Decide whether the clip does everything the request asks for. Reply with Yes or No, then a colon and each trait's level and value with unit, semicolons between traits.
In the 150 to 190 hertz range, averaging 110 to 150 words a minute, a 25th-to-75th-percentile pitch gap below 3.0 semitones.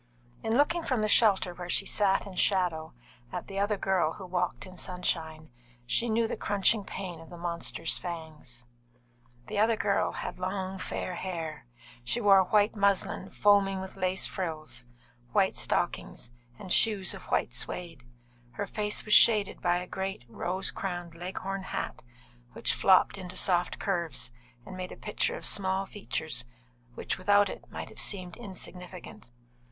No: medium, 185 Hz; average, 160 wpm; narrow, 2.5 semitones